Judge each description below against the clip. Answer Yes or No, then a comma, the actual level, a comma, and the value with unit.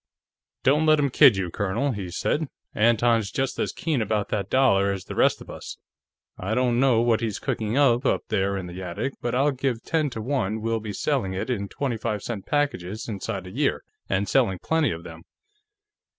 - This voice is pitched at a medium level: No, low, 115 Hz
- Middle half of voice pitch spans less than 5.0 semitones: No, average, 5.3 semitones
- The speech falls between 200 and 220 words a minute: Yes, fast, 205 wpm